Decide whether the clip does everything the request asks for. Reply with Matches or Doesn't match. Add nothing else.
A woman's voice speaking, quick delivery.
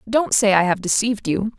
Matches